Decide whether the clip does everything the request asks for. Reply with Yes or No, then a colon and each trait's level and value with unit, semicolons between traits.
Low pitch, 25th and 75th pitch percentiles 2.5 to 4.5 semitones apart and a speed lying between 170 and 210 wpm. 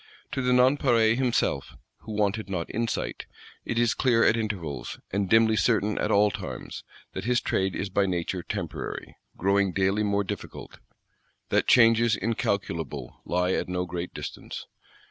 No: low, 100 Hz; average, 3.7 semitones; average, 150 wpm